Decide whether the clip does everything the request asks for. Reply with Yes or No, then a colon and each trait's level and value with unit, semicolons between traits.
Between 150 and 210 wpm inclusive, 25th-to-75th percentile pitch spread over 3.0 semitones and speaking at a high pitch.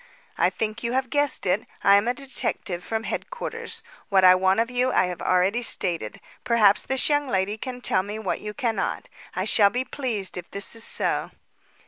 Yes: average, 195 wpm; average, 4.6 semitones; high, 220 Hz